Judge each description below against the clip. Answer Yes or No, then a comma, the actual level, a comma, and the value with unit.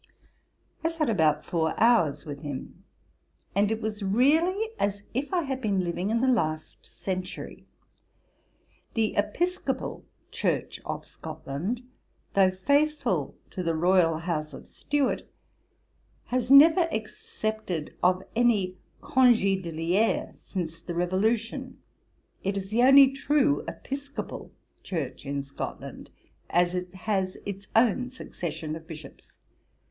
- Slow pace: Yes, slow, 120 wpm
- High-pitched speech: Yes, high, 200 Hz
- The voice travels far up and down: Yes, wide, 6.7 semitones